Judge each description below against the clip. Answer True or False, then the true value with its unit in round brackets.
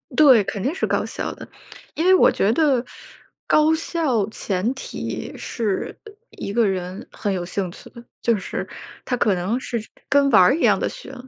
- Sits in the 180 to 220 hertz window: False (235 Hz)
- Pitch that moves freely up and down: True (6.1 semitones)